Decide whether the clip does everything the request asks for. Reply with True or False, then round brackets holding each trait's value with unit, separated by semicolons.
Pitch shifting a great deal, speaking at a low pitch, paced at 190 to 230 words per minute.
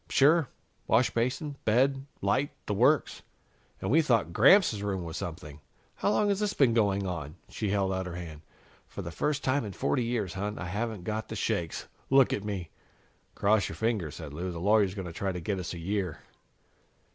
True (5.7 semitones; 105 Hz; 195 wpm)